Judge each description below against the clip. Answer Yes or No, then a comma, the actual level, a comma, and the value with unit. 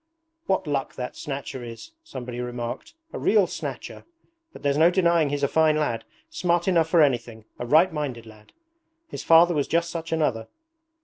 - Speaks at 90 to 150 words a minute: No, average, 175 wpm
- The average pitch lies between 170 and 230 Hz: No, medium, 150 Hz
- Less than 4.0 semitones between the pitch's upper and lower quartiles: No, wide, 5.6 semitones